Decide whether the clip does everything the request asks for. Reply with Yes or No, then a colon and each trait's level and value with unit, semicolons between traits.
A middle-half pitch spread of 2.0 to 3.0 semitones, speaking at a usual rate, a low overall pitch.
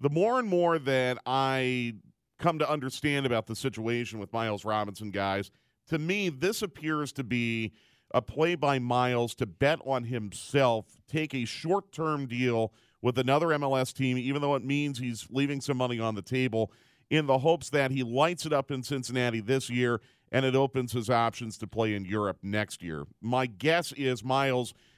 No: average, 3.8 semitones; average, 185 wpm; low, 130 Hz